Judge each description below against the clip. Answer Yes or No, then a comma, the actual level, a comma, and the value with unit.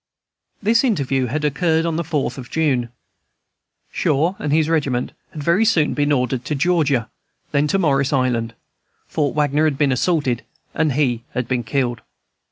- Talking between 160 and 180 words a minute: Yes, average, 165 wpm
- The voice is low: No, medium, 145 Hz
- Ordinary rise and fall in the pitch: Yes, average, 3.8 semitones